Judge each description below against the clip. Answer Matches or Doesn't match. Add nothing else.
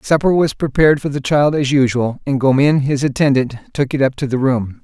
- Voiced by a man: Matches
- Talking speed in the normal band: Doesn't match